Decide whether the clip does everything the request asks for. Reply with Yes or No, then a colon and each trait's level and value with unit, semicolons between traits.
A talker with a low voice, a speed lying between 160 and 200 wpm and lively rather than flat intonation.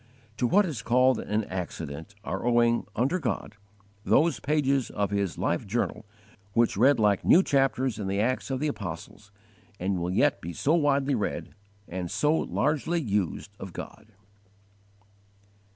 No: low, 115 Hz; average, 150 wpm; wide, 5.8 semitones